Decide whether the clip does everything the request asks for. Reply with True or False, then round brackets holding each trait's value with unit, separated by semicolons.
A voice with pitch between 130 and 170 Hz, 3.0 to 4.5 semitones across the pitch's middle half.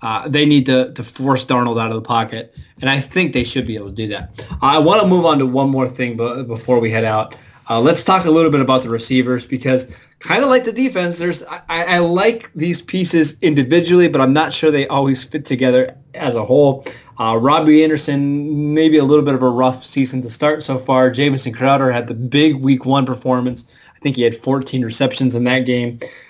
True (135 Hz; 3.7 semitones)